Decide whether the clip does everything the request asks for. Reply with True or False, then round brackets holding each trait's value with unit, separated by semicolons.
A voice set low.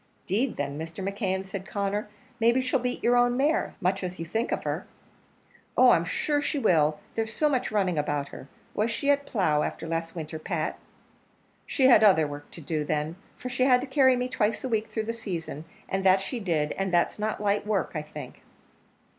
False (200 Hz)